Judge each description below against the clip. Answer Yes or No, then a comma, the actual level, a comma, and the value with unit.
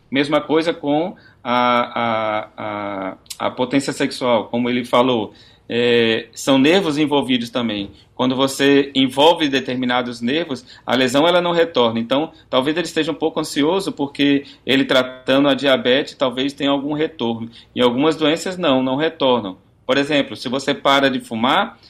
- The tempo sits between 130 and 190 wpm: Yes, average, 155 wpm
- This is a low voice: Yes, low, 130 Hz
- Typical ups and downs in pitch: Yes, average, 3.1 semitones